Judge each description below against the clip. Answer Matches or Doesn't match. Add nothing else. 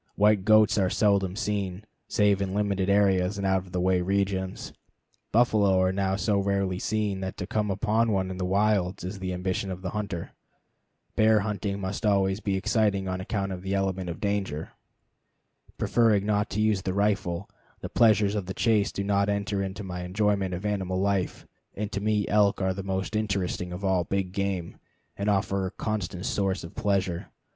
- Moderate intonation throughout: Doesn't match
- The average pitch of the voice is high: Doesn't match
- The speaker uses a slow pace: Doesn't match